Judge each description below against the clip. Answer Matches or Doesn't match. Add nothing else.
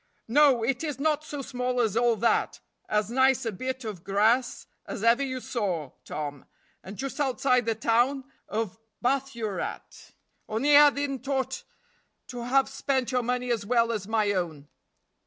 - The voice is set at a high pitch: Matches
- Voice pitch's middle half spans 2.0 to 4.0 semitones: Matches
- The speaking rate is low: Doesn't match